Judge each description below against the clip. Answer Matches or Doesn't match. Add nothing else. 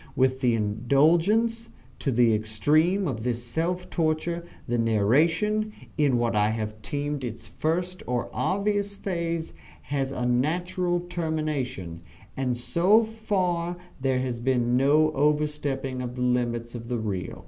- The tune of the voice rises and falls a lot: Matches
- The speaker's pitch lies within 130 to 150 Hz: Matches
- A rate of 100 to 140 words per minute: Matches